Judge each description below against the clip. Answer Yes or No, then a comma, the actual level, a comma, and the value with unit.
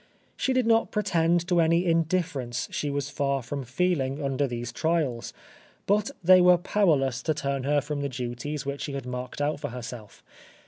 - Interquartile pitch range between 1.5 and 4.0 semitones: No, average, 4.5 semitones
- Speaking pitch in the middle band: Yes, medium, 145 Hz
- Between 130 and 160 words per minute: No, average, 180 wpm